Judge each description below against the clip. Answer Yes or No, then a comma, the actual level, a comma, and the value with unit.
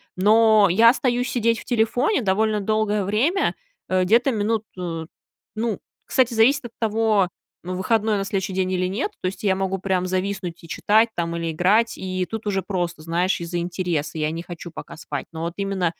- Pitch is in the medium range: No, high, 195 Hz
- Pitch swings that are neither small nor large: Yes, average, 3.5 semitones